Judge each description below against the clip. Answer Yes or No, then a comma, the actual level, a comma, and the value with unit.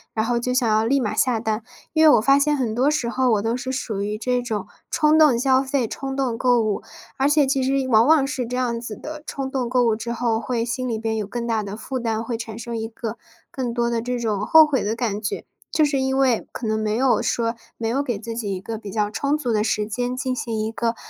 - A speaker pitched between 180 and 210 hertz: No, high, 240 Hz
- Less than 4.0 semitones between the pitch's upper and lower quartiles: Yes, average, 2.9 semitones